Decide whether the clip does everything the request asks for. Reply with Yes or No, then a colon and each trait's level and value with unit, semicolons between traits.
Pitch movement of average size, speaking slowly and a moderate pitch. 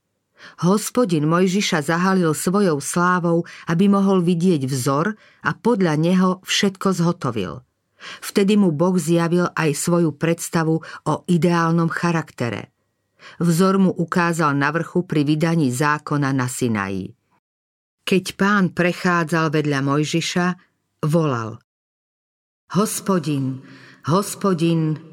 Yes: average, 3.6 semitones; slow, 100 wpm; medium, 170 Hz